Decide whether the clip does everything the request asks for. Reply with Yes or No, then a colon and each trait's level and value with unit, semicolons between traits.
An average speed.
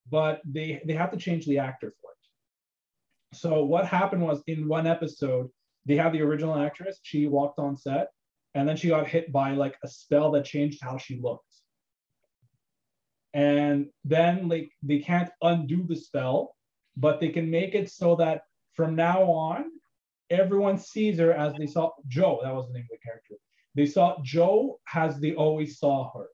Yes: average, 180 wpm